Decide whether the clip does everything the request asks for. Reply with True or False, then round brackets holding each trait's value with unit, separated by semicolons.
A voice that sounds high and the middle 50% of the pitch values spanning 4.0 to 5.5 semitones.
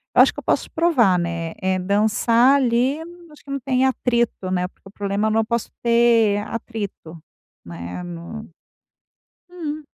True (225 Hz; 5.0 semitones)